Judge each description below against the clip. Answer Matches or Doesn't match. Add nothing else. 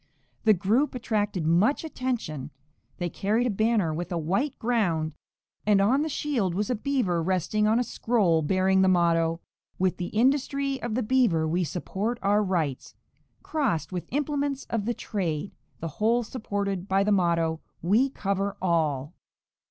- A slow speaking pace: Doesn't match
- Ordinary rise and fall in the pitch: Doesn't match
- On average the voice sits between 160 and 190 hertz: Doesn't match